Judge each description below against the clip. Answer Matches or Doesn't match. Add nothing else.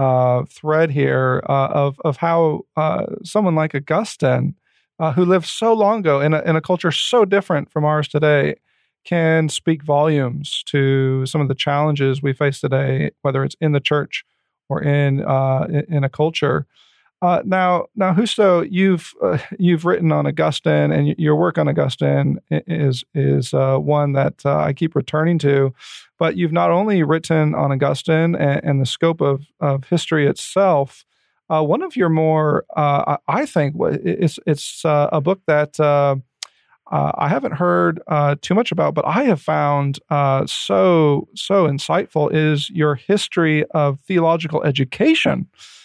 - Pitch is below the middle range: Doesn't match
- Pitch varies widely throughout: Doesn't match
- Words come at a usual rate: Matches